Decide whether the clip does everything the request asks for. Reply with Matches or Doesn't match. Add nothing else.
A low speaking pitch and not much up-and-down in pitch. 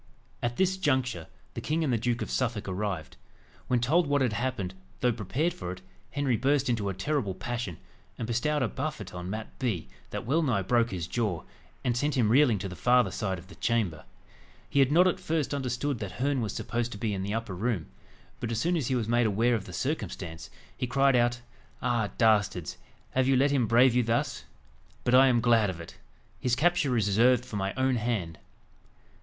Doesn't match